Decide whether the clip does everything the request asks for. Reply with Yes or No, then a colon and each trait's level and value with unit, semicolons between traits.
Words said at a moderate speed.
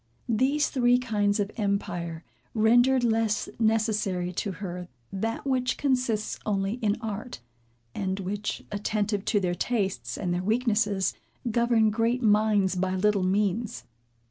No: slow, 130 wpm